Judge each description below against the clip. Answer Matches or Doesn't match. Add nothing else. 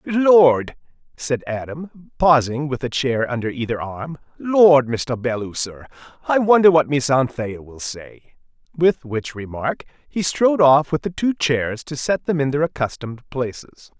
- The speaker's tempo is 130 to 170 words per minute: Matches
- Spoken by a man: Matches